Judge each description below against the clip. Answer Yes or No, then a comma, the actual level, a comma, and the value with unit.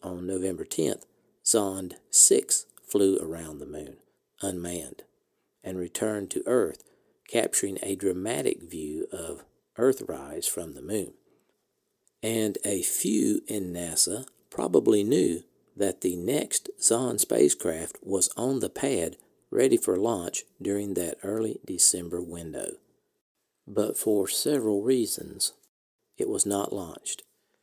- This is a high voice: No, low, 100 Hz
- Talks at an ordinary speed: No, slow, 120 wpm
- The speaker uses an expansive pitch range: Yes, wide, 8.2 semitones